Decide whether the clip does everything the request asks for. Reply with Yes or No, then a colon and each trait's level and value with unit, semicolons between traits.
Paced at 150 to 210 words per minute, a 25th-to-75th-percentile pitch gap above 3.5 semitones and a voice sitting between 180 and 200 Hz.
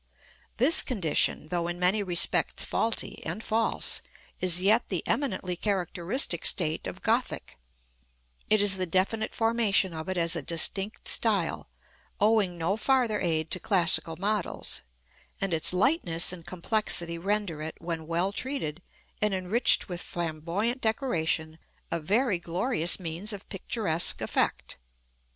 No: slow, 135 wpm; average, 4.3 semitones; medium, 185 Hz